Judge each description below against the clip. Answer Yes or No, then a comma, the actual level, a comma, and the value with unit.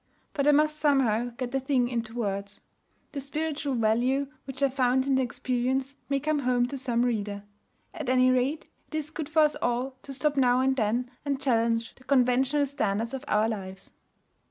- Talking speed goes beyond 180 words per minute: Yes, average, 190 wpm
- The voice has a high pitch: Yes, very high, 255 Hz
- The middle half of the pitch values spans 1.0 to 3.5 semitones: Yes, average, 2.7 semitones